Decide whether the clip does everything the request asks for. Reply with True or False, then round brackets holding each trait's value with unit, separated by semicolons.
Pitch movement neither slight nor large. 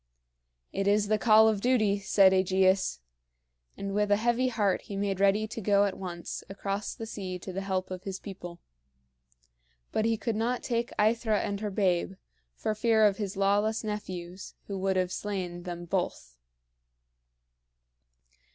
False (2.3 semitones)